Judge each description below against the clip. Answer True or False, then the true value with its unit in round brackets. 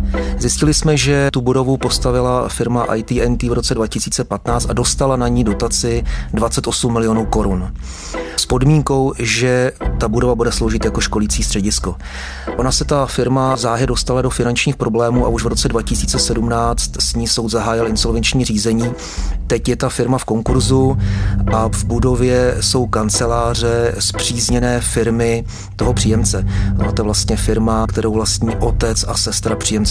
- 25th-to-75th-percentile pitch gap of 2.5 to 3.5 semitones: True (2.8 semitones)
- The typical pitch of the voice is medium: False (115 Hz)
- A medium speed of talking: True (150 wpm)